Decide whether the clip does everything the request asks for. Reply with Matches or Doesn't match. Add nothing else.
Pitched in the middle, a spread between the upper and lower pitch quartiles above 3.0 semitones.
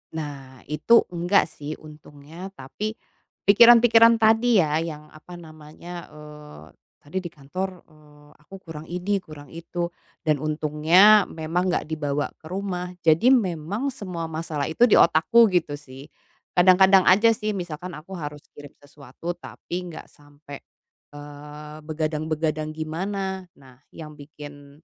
Matches